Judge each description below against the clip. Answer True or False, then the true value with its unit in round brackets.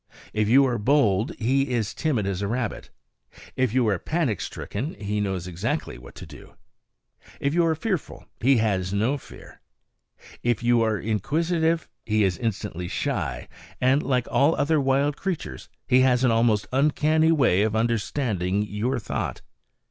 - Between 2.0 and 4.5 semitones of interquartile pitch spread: False (5.2 semitones)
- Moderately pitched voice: False (120 Hz)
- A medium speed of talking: True (160 wpm)